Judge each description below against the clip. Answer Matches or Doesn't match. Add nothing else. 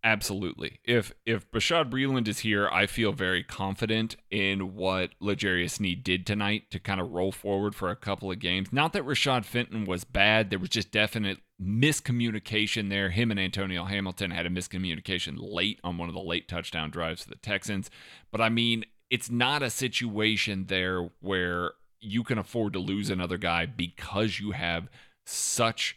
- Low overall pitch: Matches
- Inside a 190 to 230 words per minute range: Doesn't match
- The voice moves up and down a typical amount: Matches